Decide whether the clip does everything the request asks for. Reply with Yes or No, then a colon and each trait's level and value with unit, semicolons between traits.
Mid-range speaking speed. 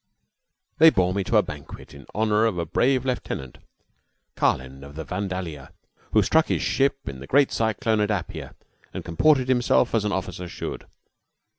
Yes: average, 175 wpm